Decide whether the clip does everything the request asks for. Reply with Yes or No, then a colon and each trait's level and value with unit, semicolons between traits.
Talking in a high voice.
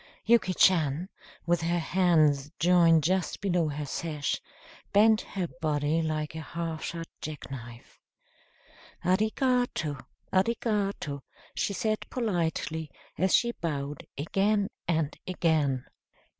No: medium, 165 Hz